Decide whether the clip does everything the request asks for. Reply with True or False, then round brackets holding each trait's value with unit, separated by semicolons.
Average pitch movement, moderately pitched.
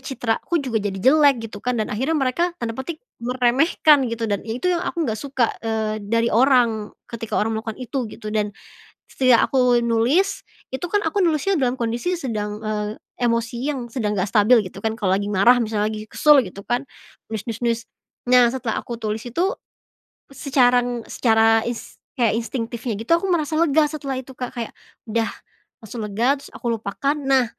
False (3.6 semitones; 240 Hz)